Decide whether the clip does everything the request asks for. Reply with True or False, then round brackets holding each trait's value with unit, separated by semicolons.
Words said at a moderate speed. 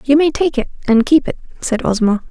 False (235 wpm)